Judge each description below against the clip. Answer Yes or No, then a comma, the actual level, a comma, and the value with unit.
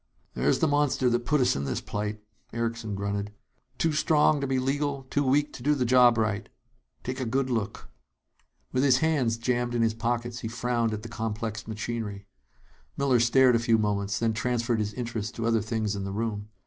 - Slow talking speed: No, average, 200 wpm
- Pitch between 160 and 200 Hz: No, low, 115 Hz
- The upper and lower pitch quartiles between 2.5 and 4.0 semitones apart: Yes, average, 2.9 semitones